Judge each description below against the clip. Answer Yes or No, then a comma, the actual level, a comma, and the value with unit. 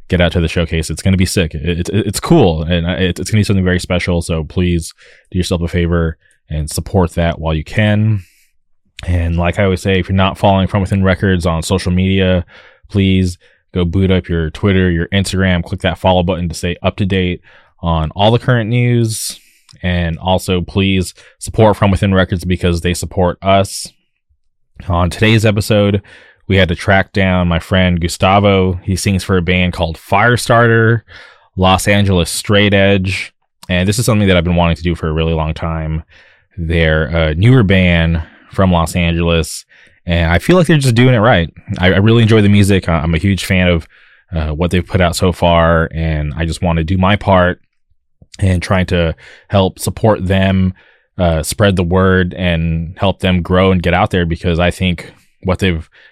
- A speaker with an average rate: Yes, average, 195 wpm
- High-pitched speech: No, very low, 90 Hz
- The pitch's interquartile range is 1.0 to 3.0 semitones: Yes, narrow, 2.4 semitones